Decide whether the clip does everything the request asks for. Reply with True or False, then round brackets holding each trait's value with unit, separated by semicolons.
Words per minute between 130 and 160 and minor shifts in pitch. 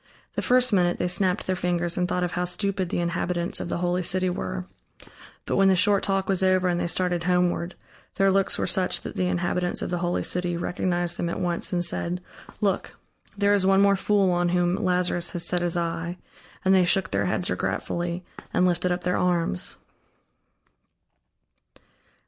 False (190 wpm; 1.2 semitones)